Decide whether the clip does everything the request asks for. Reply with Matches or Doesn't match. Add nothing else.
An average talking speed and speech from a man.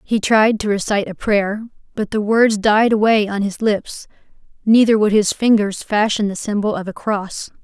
Doesn't match